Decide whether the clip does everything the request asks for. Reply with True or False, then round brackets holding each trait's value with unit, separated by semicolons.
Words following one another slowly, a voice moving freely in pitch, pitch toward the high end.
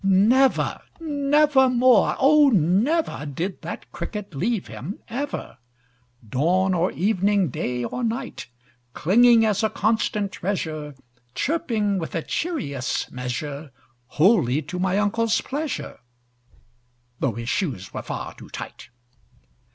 True (120 wpm; 7.6 semitones; 200 Hz)